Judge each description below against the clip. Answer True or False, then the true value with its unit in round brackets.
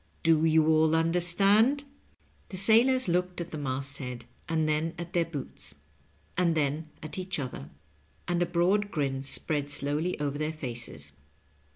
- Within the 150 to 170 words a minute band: True (160 wpm)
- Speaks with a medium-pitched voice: True (160 Hz)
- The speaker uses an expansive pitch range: False (3.6 semitones)